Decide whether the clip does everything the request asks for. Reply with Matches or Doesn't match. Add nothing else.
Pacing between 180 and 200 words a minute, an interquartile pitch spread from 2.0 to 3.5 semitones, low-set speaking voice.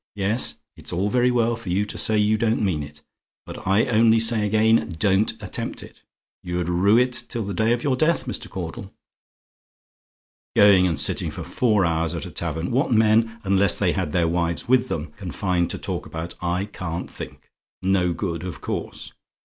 Doesn't match